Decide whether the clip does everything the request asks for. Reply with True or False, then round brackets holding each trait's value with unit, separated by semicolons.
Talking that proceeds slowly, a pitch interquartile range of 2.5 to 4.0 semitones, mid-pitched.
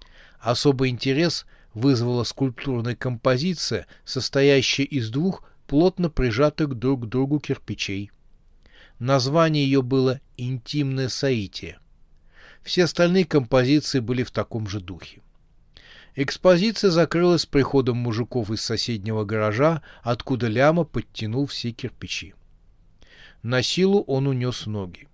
False (105 wpm; 3.7 semitones; 130 Hz)